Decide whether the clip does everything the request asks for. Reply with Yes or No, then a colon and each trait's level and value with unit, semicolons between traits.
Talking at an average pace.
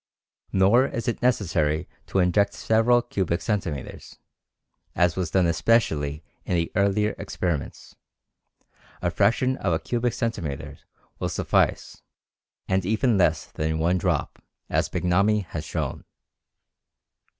No: slow, 120 wpm